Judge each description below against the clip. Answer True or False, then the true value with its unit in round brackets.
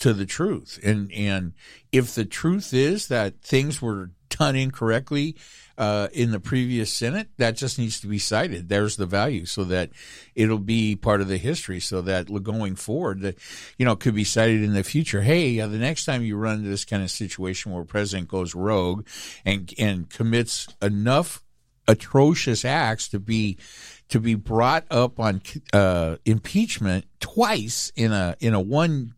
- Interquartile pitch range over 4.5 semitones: False (4.0 semitones)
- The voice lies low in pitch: True (110 Hz)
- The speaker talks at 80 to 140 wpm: False (175 wpm)